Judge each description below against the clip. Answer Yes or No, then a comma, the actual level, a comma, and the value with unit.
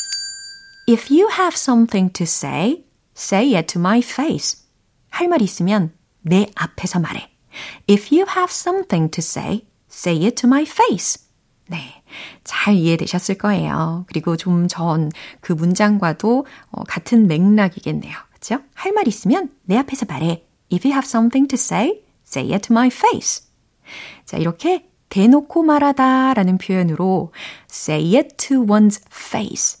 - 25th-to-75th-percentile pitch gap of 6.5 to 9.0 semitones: Yes, wide, 7.5 semitones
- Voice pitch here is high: Yes, high, 210 Hz